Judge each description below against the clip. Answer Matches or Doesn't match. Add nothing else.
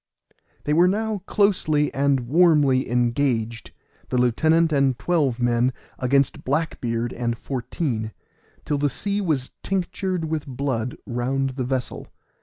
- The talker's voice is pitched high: Doesn't match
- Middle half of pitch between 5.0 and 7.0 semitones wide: Doesn't match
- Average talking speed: Doesn't match